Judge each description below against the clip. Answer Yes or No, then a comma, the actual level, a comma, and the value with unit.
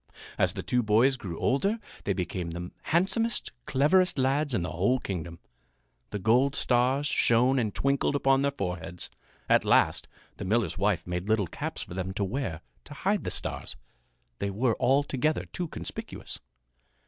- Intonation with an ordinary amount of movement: No, wide, 6.6 semitones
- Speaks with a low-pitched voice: Yes, low, 120 Hz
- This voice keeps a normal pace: Yes, average, 160 wpm